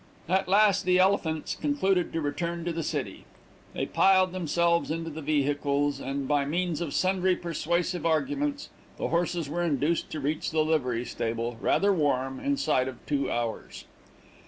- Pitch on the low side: No, medium, 165 Hz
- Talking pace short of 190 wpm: Yes, average, 160 wpm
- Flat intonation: No, average, 4.1 semitones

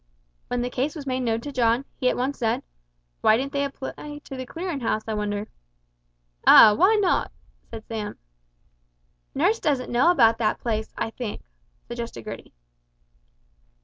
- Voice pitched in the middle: No, very high, 250 Hz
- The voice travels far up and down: No, average, 3.9 semitones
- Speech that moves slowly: No, average, 160 wpm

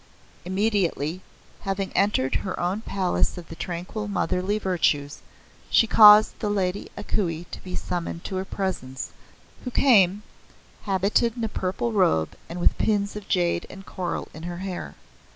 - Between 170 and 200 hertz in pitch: Yes, high, 190 Hz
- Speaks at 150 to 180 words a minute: Yes, average, 155 wpm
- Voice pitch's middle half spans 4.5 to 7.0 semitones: No, average, 2.8 semitones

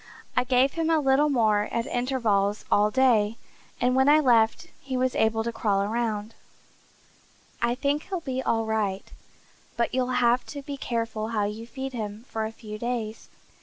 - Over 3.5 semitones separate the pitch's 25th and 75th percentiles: No, average, 3.2 semitones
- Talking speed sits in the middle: Yes, average, 175 wpm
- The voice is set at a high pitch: Yes, high, 235 Hz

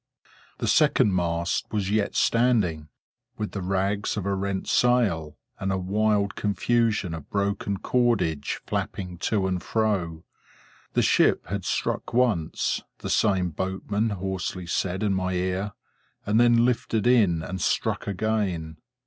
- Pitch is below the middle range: Yes, low, 100 Hz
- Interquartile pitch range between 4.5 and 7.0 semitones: No, average, 3.0 semitones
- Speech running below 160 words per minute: Yes, average, 140 wpm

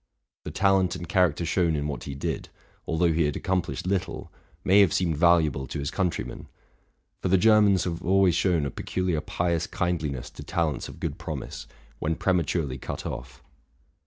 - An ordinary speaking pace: Yes, average, 175 wpm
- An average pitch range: Yes, average, 3.3 semitones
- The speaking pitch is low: Yes, very low, 85 Hz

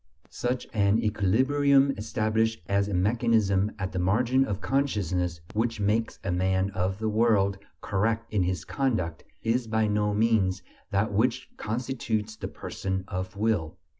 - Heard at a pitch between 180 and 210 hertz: No, low, 105 Hz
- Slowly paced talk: No, average, 145 wpm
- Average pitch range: Yes, average, 3.0 semitones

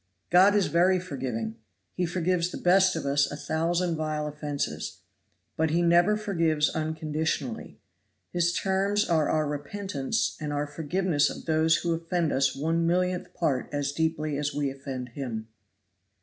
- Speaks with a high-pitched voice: No, medium, 160 Hz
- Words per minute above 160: No, average, 150 wpm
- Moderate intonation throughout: Yes, average, 3.4 semitones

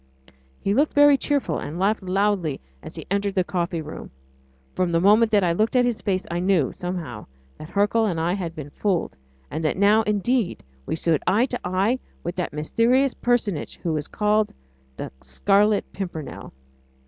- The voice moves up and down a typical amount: Yes, average, 4.1 semitones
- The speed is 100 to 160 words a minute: No, average, 180 wpm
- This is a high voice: Yes, high, 195 Hz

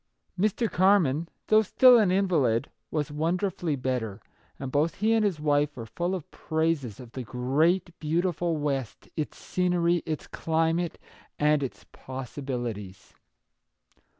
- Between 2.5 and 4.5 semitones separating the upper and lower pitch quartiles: No, average, 5.0 semitones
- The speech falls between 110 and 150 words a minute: Yes, slow, 135 wpm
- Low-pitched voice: No, medium, 155 Hz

